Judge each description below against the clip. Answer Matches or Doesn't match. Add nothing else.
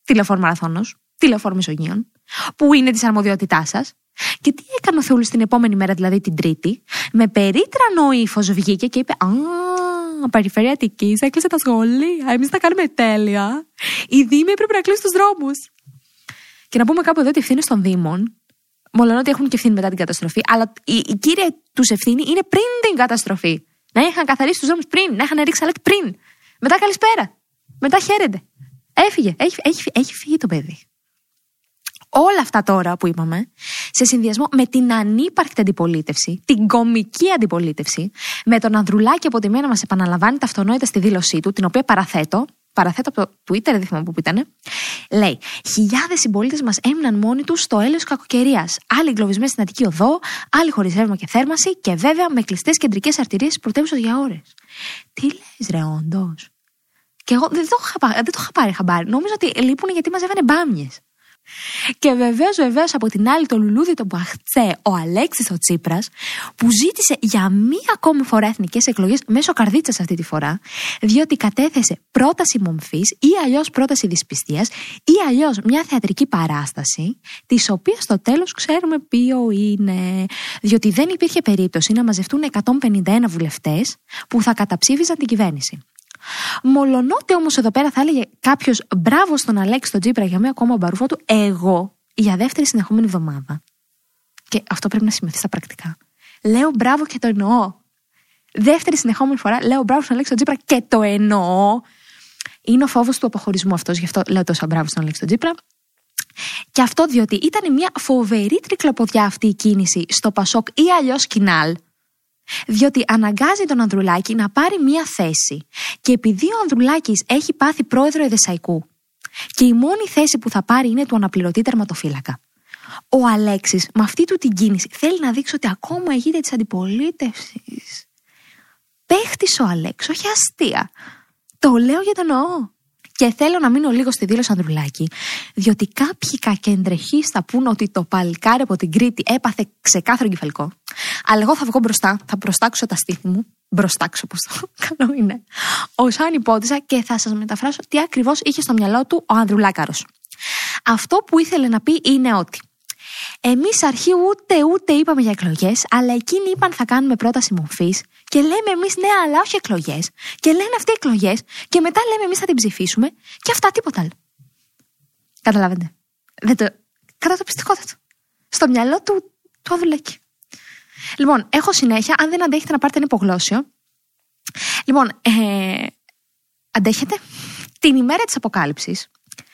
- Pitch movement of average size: Doesn't match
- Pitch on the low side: Doesn't match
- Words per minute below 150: Doesn't match